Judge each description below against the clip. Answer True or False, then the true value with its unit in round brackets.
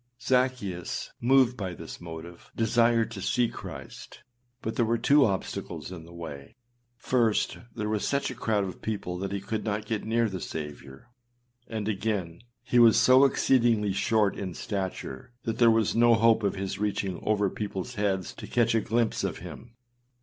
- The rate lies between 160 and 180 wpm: True (175 wpm)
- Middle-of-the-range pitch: False (110 Hz)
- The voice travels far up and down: False (3.5 semitones)